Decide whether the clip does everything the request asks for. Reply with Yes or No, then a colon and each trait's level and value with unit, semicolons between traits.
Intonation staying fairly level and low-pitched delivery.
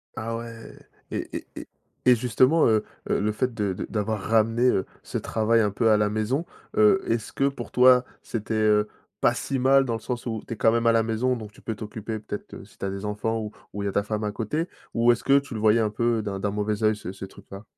Yes: narrow, 2.2 semitones; low, 110 Hz